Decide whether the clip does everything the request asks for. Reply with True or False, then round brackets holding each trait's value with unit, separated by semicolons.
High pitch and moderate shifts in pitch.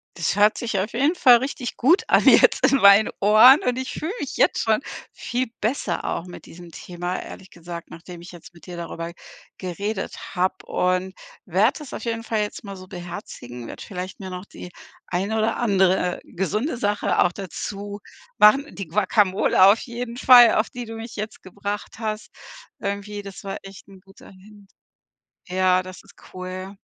True (200 Hz; 3.4 semitones)